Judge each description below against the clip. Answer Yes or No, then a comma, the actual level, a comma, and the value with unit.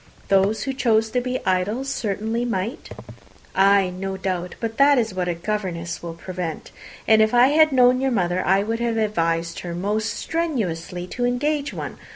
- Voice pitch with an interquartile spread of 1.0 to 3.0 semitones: No, average, 5.1 semitones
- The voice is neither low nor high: No, high, 215 Hz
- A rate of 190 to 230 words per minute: No, average, 180 wpm